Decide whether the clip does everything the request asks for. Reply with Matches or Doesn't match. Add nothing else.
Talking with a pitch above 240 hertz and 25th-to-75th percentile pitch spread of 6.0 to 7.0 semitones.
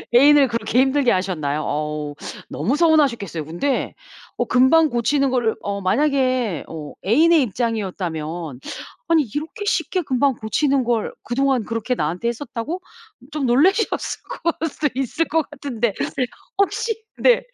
Matches